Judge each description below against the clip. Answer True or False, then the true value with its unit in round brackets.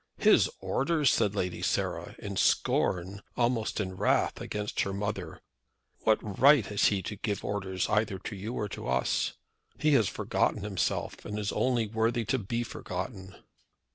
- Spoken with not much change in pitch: False (3.1 semitones)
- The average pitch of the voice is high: False (105 Hz)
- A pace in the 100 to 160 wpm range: True (155 wpm)